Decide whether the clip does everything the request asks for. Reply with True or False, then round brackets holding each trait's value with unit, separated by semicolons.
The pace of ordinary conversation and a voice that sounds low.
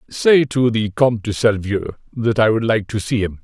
False (225 wpm; 115 Hz)